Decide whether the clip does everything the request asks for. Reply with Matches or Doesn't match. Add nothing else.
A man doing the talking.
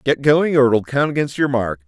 Matches